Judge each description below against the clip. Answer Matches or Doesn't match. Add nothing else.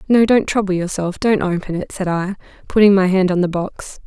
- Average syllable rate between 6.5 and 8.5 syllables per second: Doesn't match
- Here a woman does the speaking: Matches